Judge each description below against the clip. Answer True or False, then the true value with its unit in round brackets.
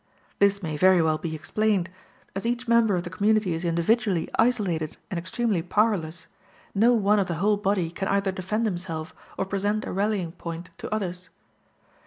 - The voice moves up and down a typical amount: True (3.8 semitones)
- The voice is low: False (195 Hz)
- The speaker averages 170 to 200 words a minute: True (175 wpm)